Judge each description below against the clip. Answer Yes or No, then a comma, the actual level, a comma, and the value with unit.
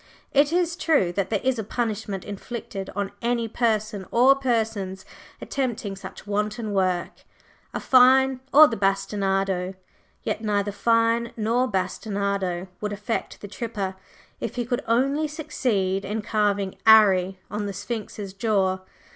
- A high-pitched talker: Yes, high, 210 Hz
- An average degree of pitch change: Yes, average, 3.5 semitones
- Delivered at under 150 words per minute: Yes, average, 140 wpm